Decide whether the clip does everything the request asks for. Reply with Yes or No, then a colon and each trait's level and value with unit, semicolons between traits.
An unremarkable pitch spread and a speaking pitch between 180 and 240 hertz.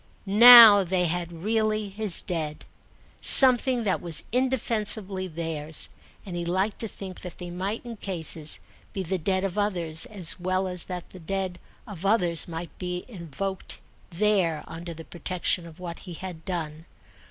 Yes: average, 3.3 semitones; medium, 185 Hz